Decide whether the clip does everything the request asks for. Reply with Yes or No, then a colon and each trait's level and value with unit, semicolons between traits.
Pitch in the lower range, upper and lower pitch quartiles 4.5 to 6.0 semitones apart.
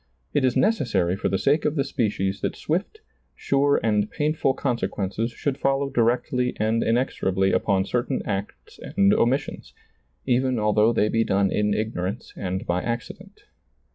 Yes: low, 115 Hz; average, 5.0 semitones